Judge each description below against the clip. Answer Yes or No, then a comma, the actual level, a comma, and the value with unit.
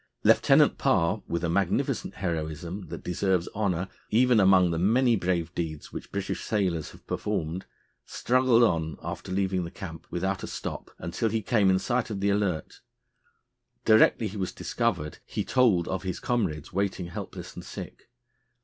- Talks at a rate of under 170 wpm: Yes, average, 160 wpm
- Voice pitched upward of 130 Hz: No, very low, 95 Hz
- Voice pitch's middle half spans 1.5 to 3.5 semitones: No, average, 3.9 semitones